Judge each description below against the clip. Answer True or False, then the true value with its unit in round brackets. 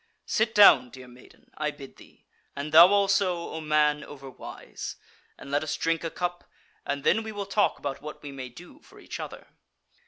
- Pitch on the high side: False (155 Hz)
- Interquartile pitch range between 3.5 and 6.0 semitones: True (4.4 semitones)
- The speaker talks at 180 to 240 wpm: True (190 wpm)